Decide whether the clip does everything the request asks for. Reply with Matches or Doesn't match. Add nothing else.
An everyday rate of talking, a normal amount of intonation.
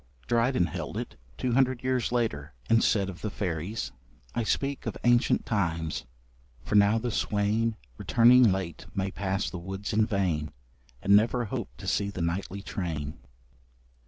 Matches